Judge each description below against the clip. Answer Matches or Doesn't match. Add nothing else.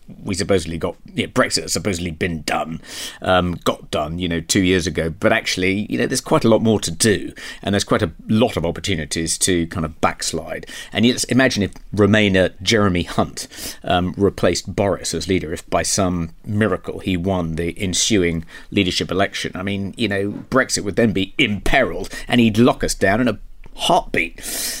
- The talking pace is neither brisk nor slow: Matches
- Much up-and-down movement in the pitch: Doesn't match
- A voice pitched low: Matches